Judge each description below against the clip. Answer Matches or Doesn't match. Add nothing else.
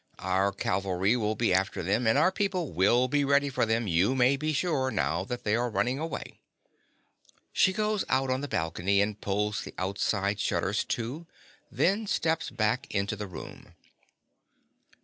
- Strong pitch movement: Matches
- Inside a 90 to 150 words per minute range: Doesn't match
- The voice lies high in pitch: Doesn't match